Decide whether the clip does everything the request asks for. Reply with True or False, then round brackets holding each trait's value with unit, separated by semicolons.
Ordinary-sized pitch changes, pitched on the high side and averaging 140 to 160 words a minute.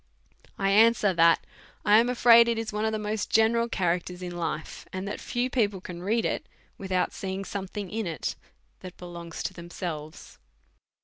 False (3.9 semitones; 195 Hz; 180 wpm)